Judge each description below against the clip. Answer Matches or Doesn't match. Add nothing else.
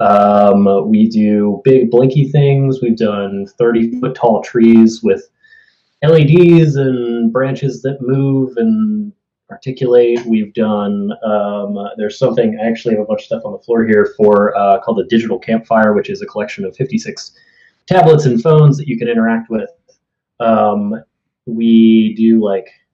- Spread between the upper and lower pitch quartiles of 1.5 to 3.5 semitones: Doesn't match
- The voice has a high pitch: Doesn't match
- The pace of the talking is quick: Doesn't match